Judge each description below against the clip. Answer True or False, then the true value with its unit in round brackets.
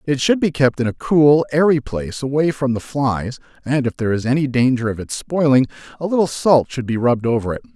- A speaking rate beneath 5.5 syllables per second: False (5.9 syllables/s)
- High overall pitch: False (135 Hz)